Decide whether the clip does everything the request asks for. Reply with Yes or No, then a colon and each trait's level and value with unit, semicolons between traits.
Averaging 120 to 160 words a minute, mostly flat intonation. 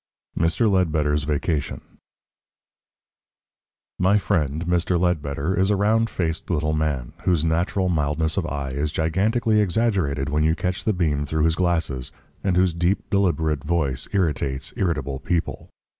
No: average, 145 wpm; average, 3.9 semitones